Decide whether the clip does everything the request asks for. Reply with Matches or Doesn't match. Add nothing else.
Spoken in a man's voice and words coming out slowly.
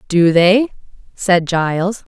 Doesn't match